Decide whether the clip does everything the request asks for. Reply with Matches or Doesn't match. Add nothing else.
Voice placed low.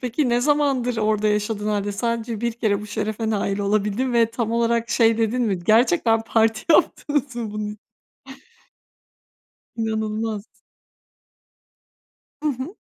Doesn't match